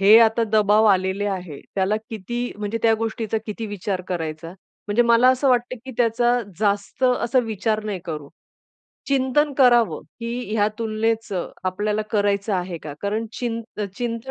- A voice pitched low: No, high, 220 Hz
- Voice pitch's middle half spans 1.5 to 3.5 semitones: Yes, average, 3.0 semitones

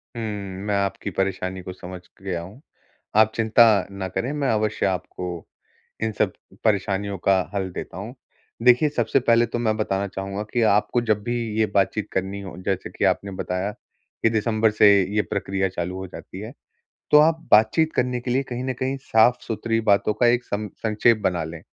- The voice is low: Yes, low, 105 Hz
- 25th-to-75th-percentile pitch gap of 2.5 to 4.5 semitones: Yes, average, 3.4 semitones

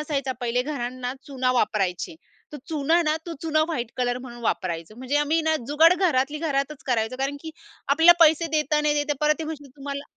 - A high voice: Yes, very high, 285 Hz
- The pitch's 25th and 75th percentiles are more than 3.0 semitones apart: Yes, average, 3.5 semitones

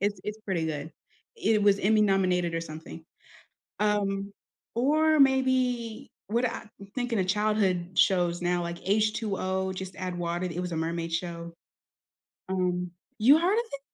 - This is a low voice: No, high, 190 Hz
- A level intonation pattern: No, average, 3.8 semitones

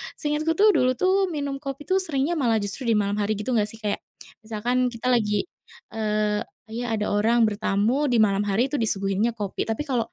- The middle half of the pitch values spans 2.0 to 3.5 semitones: No, average, 4.6 semitones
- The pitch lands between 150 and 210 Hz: No, high, 230 Hz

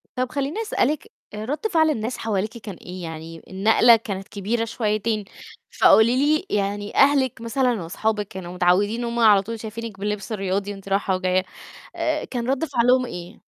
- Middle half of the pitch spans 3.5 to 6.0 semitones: Yes, average, 3.9 semitones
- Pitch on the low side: No, high, 220 Hz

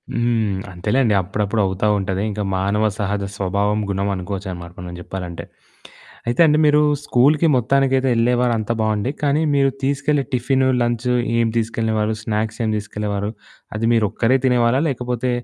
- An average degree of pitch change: Yes, average, 3.7 semitones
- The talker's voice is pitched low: Yes, low, 110 Hz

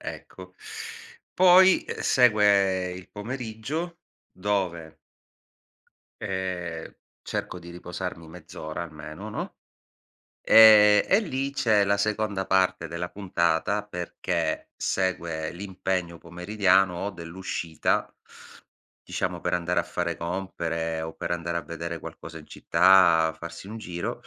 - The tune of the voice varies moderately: Yes, average, 3.4 semitones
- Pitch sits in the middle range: No, very low, 90 Hz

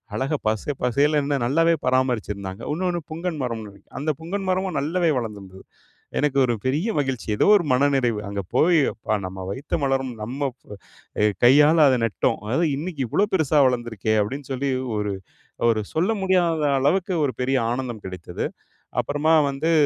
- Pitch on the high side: No, low, 135 Hz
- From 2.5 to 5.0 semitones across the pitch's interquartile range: No, wide, 5.6 semitones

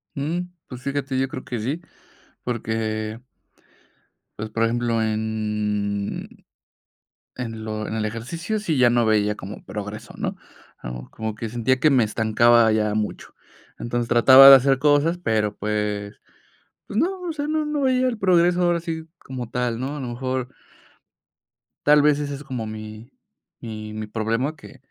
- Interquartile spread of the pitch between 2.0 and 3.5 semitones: No, average, 4.9 semitones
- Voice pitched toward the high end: No, low, 120 Hz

